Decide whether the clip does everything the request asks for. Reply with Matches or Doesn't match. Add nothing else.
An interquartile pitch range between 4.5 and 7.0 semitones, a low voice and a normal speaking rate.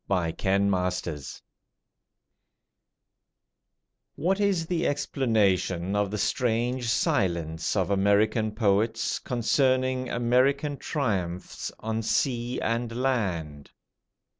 Doesn't match